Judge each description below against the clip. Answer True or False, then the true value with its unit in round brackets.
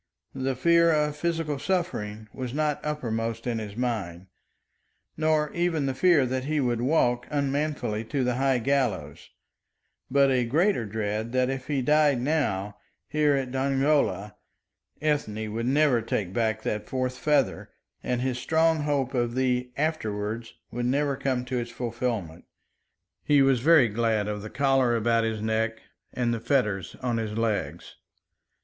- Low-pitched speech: True (125 Hz)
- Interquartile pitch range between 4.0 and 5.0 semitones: True (4.3 semitones)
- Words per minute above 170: False (155 wpm)